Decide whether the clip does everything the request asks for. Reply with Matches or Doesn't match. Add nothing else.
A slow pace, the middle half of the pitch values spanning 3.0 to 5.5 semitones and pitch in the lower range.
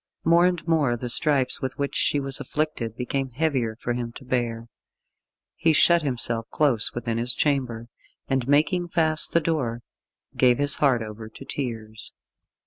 Doesn't match